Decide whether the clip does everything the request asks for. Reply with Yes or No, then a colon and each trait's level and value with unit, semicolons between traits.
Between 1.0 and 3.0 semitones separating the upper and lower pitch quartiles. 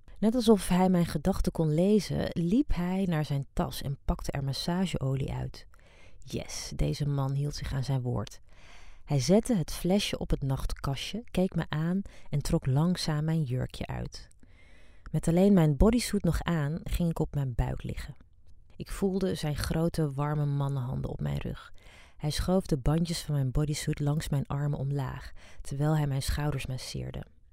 No: average, 4.5 semitones